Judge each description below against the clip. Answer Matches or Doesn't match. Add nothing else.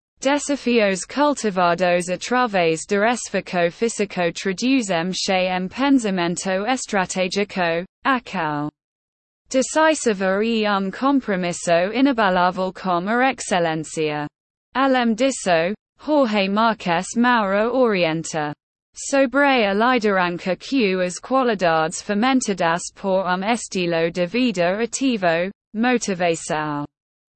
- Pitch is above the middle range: Matches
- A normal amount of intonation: Doesn't match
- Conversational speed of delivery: Doesn't match